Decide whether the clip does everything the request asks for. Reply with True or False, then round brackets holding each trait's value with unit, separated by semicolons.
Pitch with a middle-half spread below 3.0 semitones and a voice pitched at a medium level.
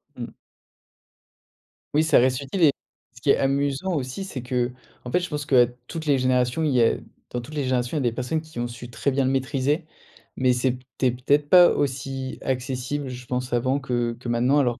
False (2.5 semitones; 130 Hz)